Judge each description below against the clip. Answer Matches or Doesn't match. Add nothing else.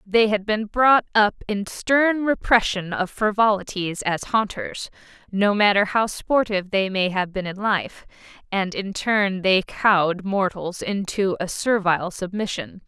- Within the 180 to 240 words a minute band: Doesn't match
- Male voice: Doesn't match